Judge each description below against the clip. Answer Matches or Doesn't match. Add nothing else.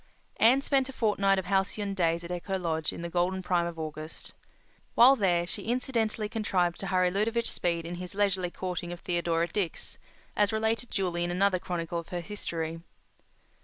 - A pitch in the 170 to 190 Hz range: Matches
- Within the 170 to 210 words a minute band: Matches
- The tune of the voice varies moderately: Matches